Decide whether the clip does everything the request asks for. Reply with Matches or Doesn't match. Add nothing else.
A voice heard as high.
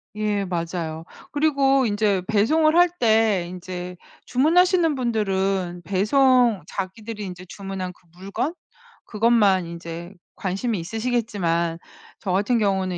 Matches